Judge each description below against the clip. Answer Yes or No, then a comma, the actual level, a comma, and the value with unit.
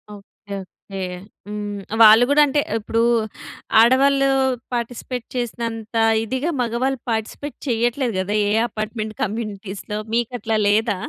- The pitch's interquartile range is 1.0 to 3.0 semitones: Yes, average, 2.7 semitones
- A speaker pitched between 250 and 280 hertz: No, high, 225 Hz